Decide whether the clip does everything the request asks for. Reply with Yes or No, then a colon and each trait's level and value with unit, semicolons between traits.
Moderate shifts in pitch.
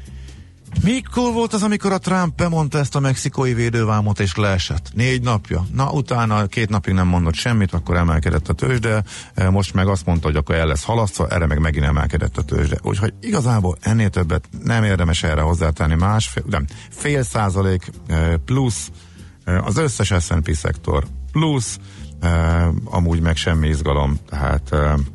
No: wide, 5.9 semitones